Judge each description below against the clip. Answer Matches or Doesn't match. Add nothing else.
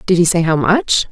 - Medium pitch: Matches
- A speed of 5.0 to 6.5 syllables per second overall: Matches